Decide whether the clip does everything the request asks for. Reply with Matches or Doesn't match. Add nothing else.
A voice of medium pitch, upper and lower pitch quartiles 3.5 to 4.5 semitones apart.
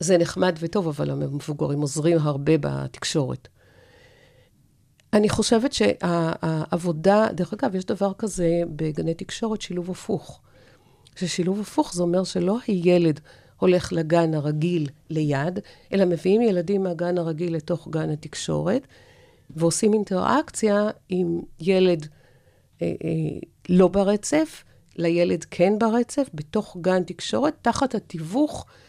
Matches